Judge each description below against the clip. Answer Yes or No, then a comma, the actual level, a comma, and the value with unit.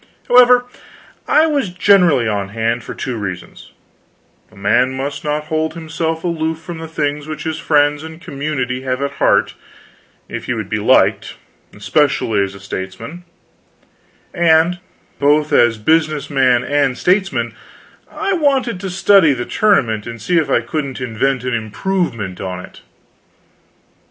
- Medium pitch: Yes, medium, 150 Hz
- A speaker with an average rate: Yes, average, 150 wpm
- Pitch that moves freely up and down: Yes, wide, 6.0 semitones